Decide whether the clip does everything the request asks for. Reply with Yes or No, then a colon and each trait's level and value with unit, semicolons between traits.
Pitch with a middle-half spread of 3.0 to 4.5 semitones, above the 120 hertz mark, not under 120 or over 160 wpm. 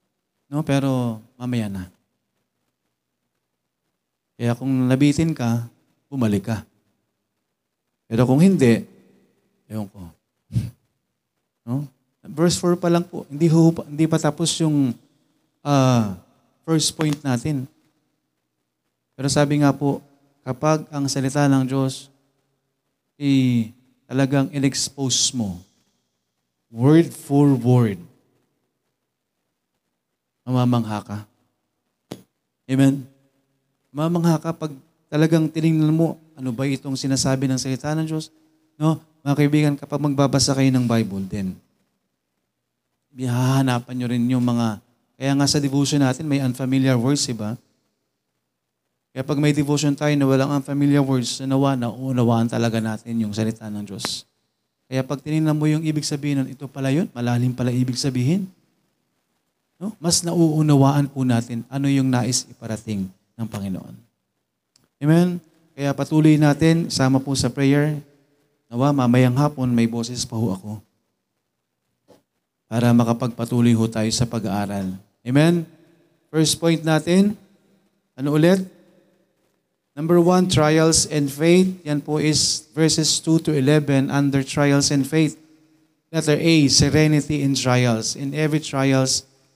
Yes: average, 4.2 semitones; low, 135 Hz; average, 125 wpm